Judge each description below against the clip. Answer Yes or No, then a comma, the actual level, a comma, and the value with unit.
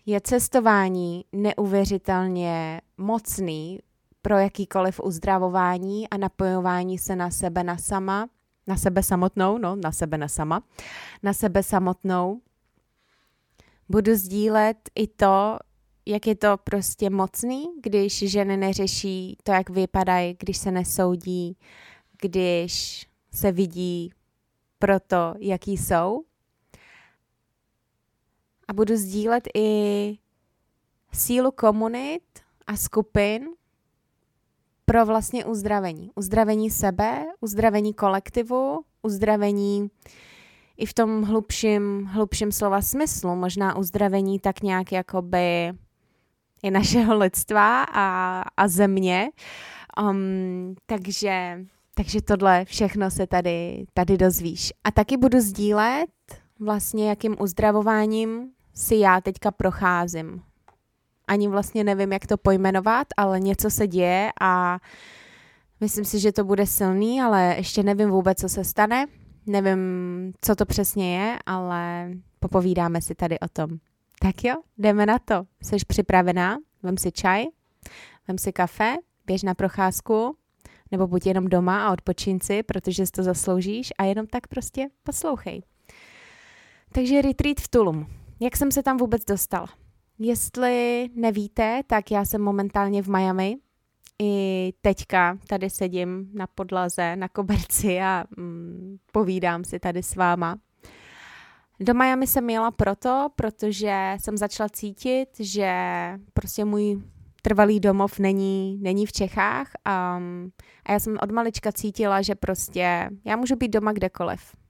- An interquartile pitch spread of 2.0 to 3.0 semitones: Yes, narrow, 2.5 semitones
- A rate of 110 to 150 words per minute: Yes, average, 125 wpm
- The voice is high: Yes, high, 195 Hz